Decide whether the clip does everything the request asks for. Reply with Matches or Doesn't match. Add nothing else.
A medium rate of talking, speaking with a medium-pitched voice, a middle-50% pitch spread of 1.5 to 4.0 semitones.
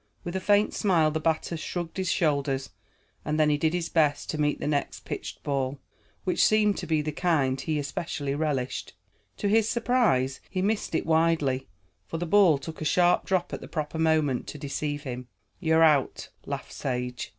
Matches